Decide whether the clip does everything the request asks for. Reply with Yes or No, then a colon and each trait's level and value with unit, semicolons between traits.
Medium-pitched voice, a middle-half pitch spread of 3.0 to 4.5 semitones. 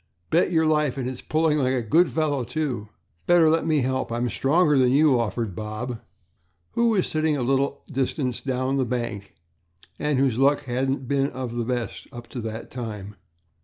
No: low, 130 Hz; average, 3.8 semitones